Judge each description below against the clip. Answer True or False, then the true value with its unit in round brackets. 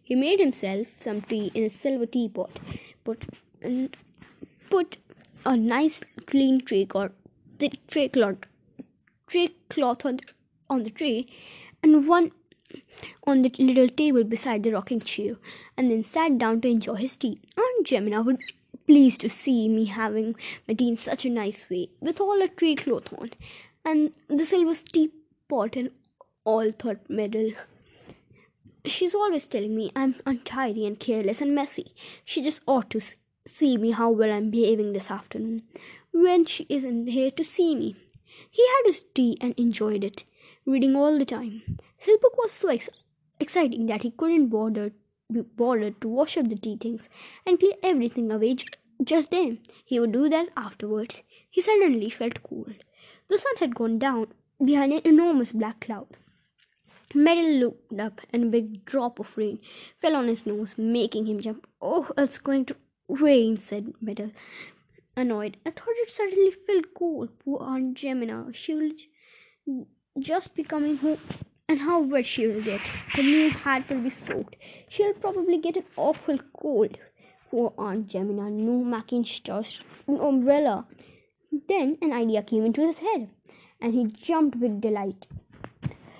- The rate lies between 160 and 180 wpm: True (165 wpm)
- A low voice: False (255 Hz)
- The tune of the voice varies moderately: False (5.8 semitones)